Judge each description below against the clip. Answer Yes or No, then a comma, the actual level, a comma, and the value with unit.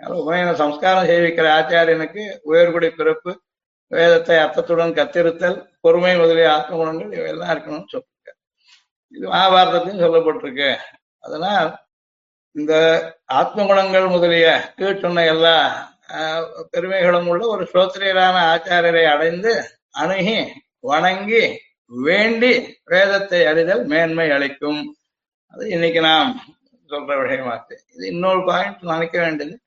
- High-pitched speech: No, medium, 170 Hz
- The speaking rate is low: No, average, 100 wpm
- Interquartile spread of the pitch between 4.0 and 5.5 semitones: No, narrow, 2.5 semitones